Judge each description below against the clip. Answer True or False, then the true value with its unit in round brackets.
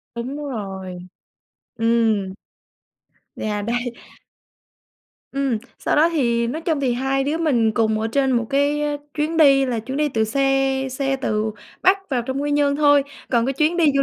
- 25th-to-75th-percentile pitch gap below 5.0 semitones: True (3.8 semitones)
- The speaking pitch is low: False (270 Hz)